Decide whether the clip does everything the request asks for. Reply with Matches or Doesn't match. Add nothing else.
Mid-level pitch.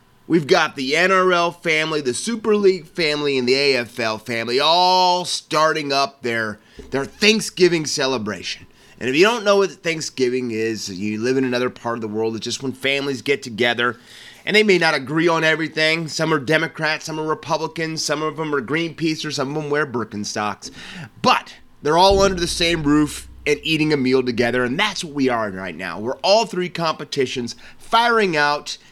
Matches